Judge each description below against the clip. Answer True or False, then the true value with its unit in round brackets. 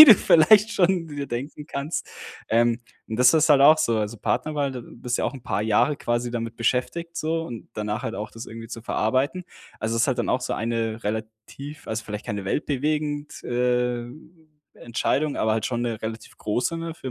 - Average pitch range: True (4.8 semitones)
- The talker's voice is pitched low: True (125 Hz)